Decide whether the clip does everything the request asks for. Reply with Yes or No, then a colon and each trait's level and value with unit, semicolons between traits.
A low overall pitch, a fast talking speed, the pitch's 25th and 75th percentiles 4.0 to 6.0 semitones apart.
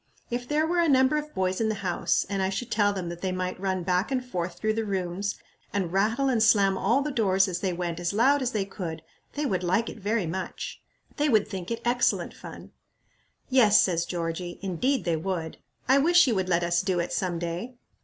No: high, 195 Hz; fast, 225 wpm; average, 5.2 semitones